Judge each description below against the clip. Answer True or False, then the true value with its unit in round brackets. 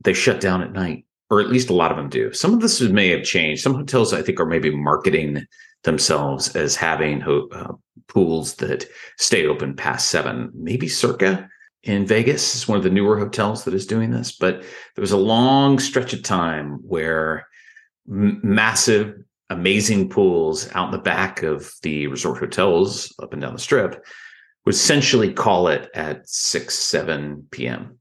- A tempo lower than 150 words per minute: False (180 wpm)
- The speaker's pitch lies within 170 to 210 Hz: False (105 Hz)